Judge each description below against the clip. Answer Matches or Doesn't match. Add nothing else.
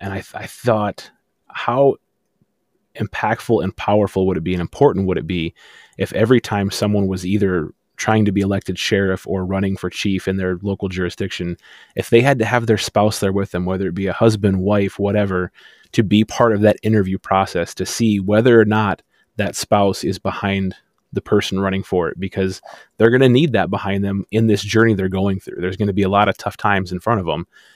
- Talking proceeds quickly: Matches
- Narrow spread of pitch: Matches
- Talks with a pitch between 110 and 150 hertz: Doesn't match